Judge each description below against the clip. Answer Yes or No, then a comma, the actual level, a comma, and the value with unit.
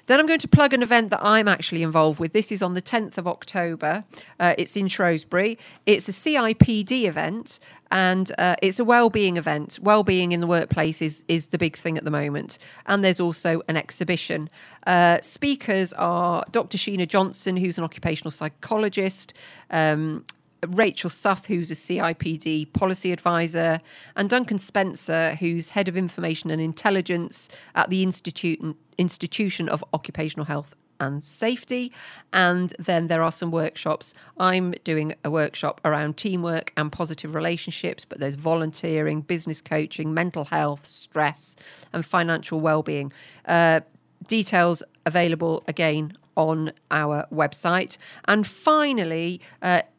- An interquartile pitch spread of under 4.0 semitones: Yes, average, 3.2 semitones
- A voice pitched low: No, medium, 170 Hz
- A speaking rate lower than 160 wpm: Yes, average, 145 wpm